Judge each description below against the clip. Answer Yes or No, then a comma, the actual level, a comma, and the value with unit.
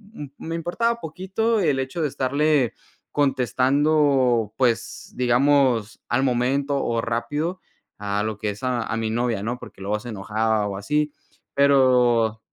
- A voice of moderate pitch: No, low, 125 Hz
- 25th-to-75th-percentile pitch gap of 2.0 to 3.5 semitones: No, average, 4.3 semitones